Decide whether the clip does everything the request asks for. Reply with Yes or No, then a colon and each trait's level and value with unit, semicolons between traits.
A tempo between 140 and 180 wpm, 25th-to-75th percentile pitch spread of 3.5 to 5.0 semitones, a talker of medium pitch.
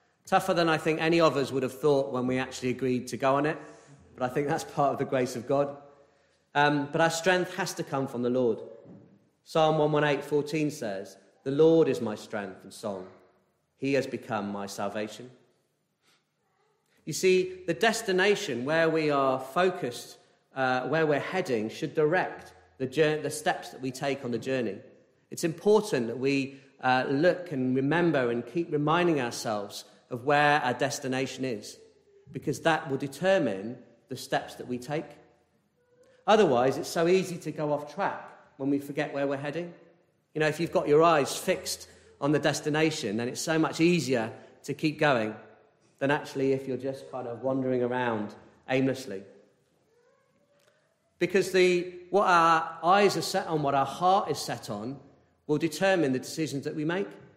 Yes: average, 175 wpm; average, 4.2 semitones; medium, 145 Hz